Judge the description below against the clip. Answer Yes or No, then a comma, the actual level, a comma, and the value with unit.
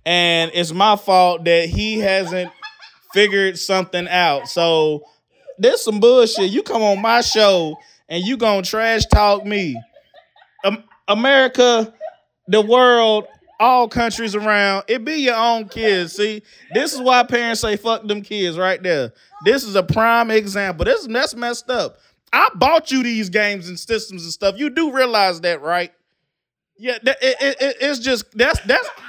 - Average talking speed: Yes, average, 160 wpm